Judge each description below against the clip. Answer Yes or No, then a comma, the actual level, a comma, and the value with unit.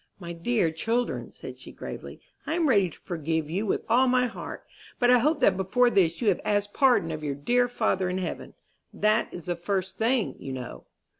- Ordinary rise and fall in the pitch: No, wide, 6.2 semitones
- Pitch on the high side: Yes, high, 200 Hz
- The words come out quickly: Yes, fast, 210 wpm